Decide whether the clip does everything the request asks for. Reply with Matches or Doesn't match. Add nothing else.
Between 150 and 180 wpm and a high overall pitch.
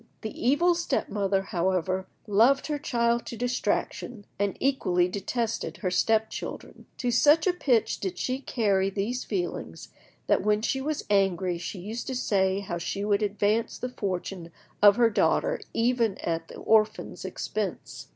Matches